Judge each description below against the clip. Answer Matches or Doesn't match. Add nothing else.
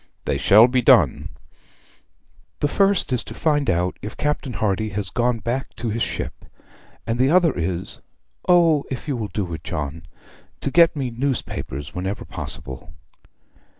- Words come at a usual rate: Matches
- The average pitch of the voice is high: Doesn't match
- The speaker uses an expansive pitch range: Matches